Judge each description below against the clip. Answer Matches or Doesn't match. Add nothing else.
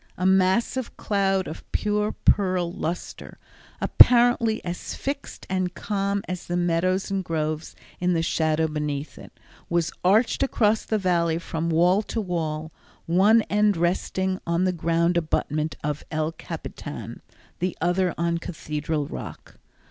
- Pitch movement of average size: Matches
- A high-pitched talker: Doesn't match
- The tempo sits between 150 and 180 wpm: Doesn't match